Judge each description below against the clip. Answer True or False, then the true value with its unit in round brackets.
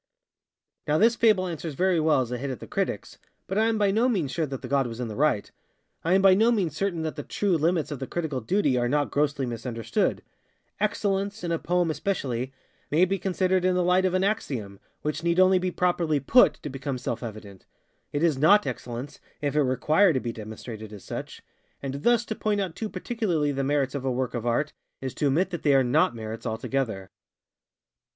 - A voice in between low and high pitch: True (150 Hz)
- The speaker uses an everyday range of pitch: False (6.4 semitones)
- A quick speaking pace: True (215 wpm)